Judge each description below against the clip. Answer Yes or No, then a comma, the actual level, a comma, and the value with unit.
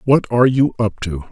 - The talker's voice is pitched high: No, low, 115 Hz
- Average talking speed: No, fast, 230 wpm